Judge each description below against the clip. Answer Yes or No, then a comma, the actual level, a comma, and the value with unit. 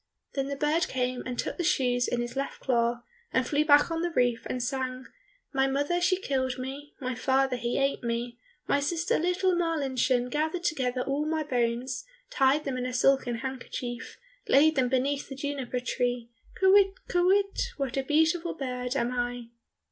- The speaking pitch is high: Yes, very high, 270 Hz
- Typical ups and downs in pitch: Yes, average, 3.5 semitones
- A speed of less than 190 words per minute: Yes, average, 180 wpm